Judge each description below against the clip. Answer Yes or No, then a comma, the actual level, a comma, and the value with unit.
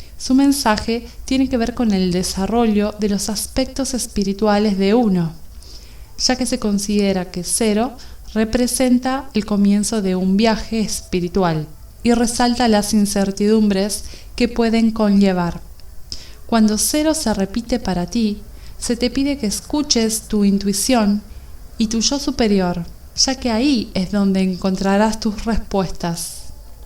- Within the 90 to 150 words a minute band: Yes, average, 130 wpm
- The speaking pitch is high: Yes, high, 215 Hz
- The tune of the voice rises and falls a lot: No, average, 3.4 semitones